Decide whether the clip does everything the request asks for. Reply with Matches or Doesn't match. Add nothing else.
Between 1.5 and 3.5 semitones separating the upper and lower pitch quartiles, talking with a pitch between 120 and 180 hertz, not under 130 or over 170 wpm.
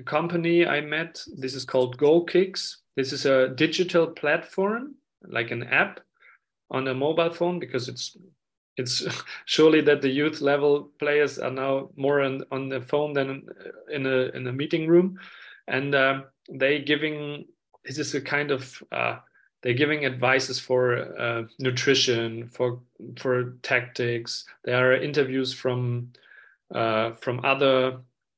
Matches